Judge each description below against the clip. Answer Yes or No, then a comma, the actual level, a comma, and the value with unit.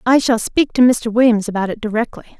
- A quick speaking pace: Yes, fast, 225 wpm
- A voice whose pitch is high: Yes, high, 230 Hz